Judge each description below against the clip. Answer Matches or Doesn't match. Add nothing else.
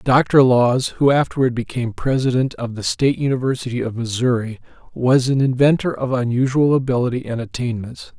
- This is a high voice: Doesn't match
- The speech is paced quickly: Doesn't match